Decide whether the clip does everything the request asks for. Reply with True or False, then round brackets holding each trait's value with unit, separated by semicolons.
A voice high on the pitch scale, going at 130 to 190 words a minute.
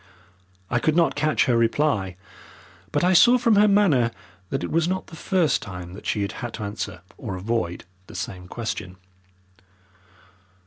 False (120 Hz; 170 wpm)